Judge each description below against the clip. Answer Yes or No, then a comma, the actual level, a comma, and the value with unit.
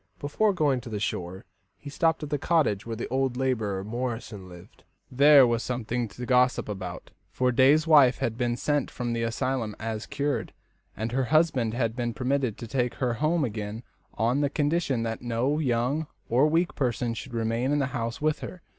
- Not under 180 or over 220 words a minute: Yes, average, 190 wpm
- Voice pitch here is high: No, low, 125 Hz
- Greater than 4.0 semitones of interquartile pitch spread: No, average, 3.7 semitones